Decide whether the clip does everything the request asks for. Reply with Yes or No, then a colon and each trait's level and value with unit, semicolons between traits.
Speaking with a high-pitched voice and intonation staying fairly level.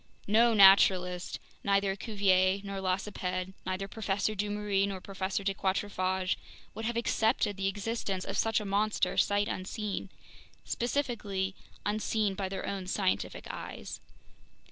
Yes: high, 195 Hz; narrow, 1.7 semitones